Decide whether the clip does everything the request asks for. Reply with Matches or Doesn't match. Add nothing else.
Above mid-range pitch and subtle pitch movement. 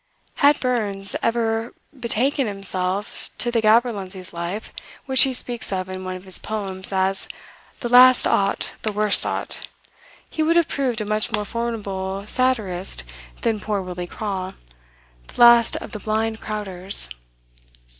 Doesn't match